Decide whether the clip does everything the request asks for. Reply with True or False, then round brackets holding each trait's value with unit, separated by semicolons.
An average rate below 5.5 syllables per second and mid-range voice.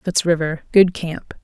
True (4.2 syllables/s; 170 Hz)